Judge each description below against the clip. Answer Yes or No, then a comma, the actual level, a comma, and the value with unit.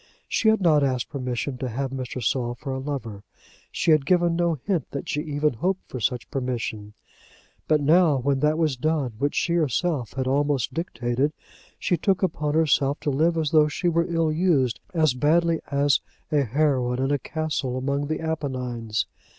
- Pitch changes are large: No, average, 3.8 semitones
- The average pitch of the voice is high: No, medium, 145 Hz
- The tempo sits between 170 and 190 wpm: Yes, average, 185 wpm